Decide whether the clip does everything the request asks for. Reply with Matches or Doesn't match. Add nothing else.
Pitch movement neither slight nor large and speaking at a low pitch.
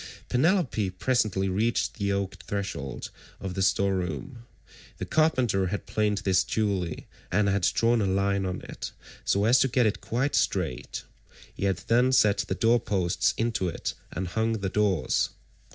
Matches